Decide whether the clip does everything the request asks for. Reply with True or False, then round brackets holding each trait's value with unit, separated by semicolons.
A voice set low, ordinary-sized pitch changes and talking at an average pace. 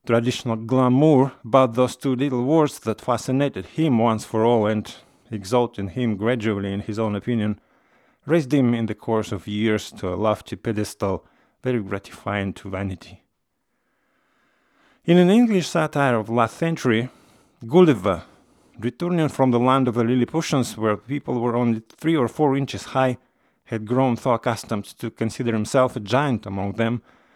True (120 Hz; 3.4 semitones; 160 wpm)